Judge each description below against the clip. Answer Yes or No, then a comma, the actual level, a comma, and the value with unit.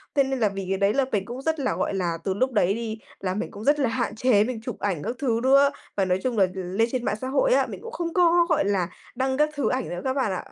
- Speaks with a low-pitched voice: No, high, 240 Hz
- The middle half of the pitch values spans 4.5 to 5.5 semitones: Yes, average, 5.2 semitones